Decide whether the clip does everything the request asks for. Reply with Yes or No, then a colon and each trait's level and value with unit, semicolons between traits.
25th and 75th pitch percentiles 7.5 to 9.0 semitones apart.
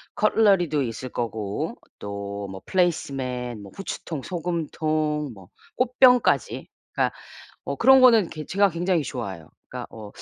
Yes: wide, 8.3 semitones